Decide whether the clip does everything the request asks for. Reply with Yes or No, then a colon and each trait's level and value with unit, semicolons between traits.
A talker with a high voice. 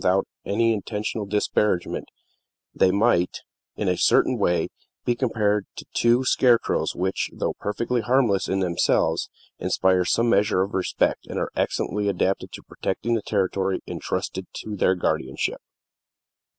No: low, 100 Hz